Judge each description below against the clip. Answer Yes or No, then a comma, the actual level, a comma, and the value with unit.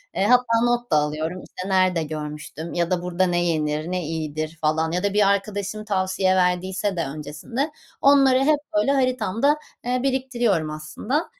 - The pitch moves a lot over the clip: Yes, wide, 6.9 semitones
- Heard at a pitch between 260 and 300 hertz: No, medium, 185 Hz